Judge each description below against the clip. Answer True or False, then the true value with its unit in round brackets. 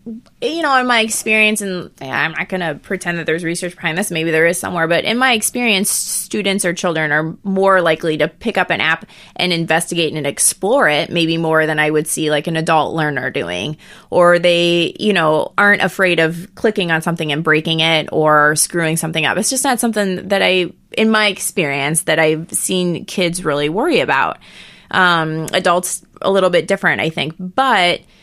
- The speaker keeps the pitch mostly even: False (3.5 semitones)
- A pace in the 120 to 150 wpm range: False (200 wpm)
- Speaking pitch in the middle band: True (170 Hz)